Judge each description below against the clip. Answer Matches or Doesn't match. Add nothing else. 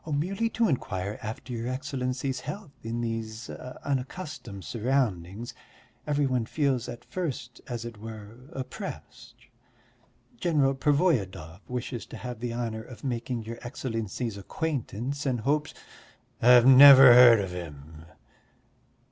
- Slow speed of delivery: Matches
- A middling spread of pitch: Matches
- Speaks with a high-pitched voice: Doesn't match